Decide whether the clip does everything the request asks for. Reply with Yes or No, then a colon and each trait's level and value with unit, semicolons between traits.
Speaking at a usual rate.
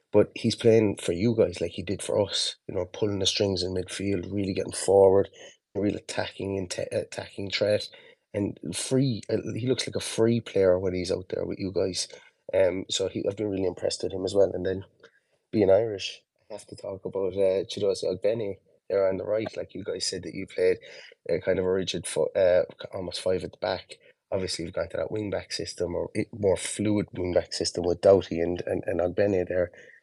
No: fast, 220 wpm